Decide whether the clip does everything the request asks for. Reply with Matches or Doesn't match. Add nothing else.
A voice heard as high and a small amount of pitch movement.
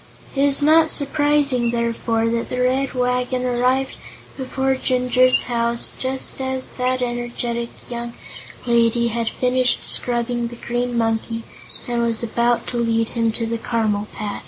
Matches